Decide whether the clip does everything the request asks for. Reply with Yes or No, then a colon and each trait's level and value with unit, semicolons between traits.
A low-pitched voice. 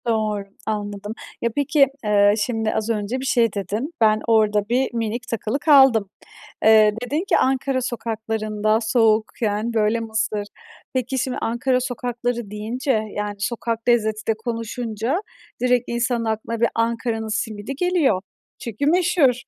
No: high, 230 Hz